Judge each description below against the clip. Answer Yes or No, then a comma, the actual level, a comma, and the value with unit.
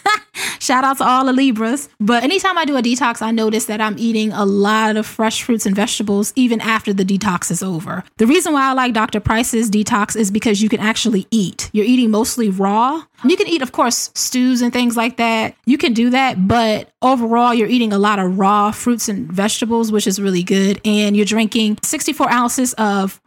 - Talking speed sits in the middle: No, fast, 215 wpm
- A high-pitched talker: Yes, high, 225 Hz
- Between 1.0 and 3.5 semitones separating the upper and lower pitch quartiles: Yes, average, 2.9 semitones